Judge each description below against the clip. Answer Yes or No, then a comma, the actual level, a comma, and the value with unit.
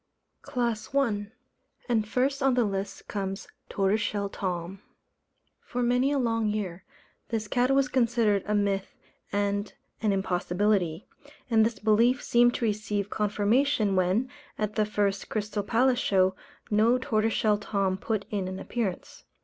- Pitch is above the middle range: Yes, high, 210 Hz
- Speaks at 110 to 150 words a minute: Yes, average, 140 wpm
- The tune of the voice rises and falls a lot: No, average, 2.9 semitones